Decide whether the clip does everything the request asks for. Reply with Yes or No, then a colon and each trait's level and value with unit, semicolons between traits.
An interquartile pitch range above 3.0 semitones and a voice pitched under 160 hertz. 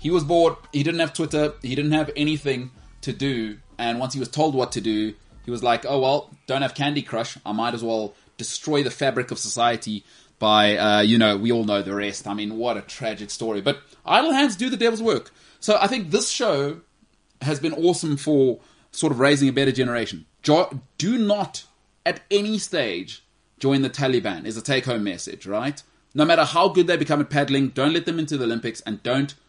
Yes: average, 4.9 semitones; low, 135 Hz